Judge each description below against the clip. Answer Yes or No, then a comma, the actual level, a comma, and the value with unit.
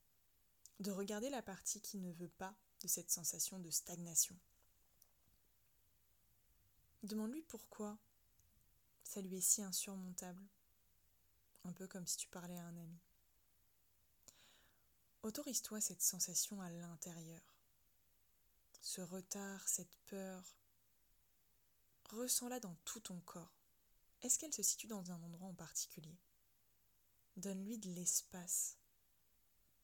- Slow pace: Yes, slow, 110 wpm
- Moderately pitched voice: Yes, medium, 175 Hz